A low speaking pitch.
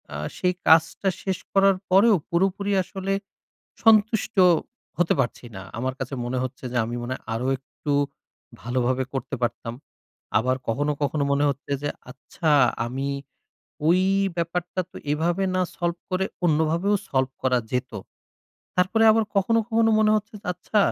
No: medium, 165 Hz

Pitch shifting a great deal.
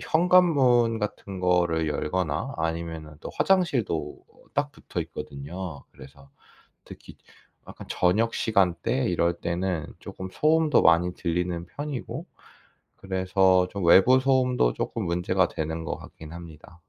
Yes: wide, 6.0 semitones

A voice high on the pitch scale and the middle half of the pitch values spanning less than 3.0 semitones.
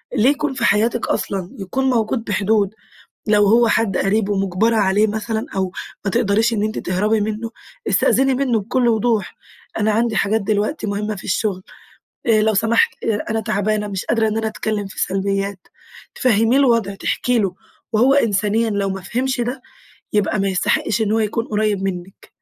Yes: high, 215 Hz; narrow, 2.4 semitones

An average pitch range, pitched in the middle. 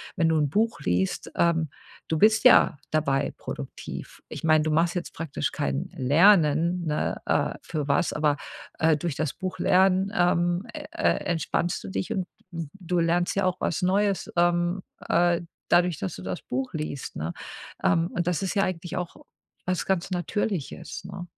Yes: average, 3.1 semitones; medium, 170 Hz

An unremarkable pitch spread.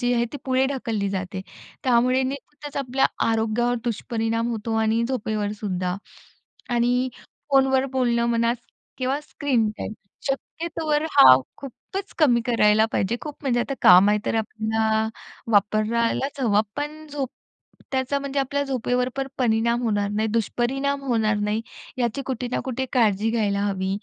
Yes: average, 3.5 semitones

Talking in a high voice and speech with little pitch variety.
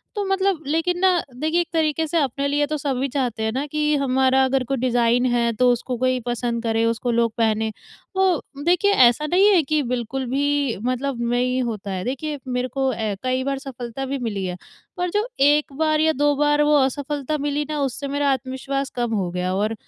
No: very high, 270 Hz; average, 3.6 semitones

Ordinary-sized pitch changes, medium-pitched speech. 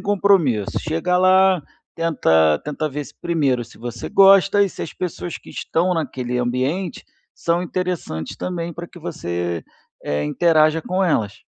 No: wide, 6.6 semitones; medium, 165 Hz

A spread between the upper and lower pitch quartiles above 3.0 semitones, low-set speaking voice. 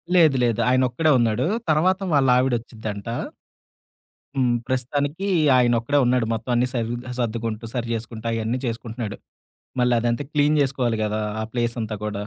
No: narrow, 2.4 semitones; low, 120 Hz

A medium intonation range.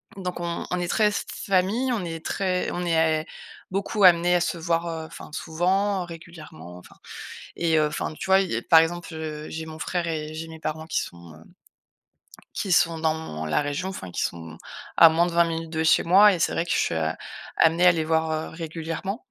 No: narrow, 2.1 semitones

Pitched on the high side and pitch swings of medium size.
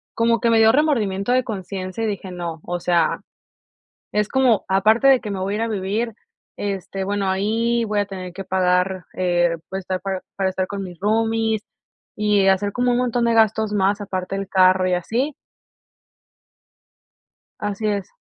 Yes: high, 200 Hz; average, 3.1 semitones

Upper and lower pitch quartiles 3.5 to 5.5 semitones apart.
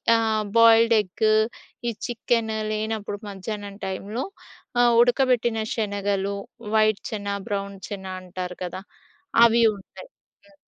No: narrow, 2.5 semitones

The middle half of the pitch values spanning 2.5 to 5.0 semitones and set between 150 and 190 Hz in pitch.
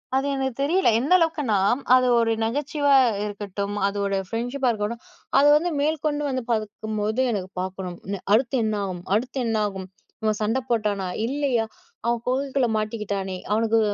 No: average, 4.6 semitones; high, 225 Hz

